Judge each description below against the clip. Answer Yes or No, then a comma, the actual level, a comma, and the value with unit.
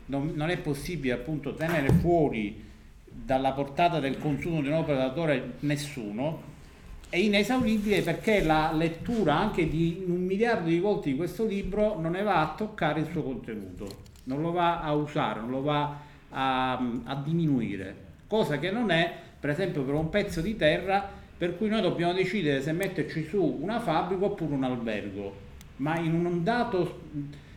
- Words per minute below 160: No, average, 165 wpm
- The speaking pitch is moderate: Yes, medium, 155 Hz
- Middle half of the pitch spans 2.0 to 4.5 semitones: No, average, 4.9 semitones